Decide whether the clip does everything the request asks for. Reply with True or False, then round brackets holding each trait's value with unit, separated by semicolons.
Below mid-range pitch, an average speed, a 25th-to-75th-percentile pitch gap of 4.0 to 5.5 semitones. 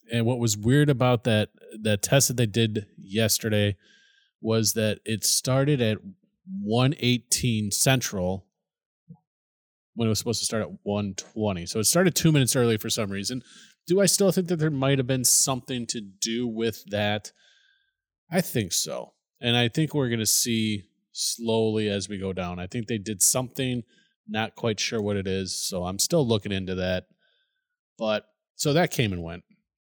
True (115 Hz; 175 wpm; 4.8 semitones)